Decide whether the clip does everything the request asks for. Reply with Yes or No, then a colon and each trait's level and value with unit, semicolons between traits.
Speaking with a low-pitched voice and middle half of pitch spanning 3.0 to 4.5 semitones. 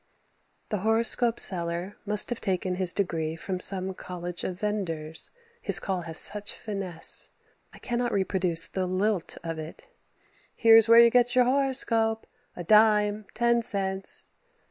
No: high, 195 Hz; average, 3.9 semitones